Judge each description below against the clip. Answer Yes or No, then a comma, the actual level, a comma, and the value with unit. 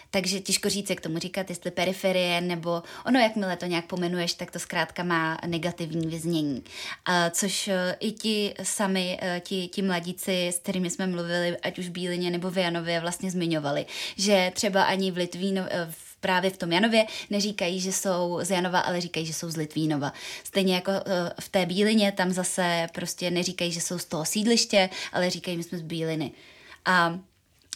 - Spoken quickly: Yes, fast, 175 wpm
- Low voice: No, medium, 180 Hz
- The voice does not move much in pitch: Yes, narrow, 1.9 semitones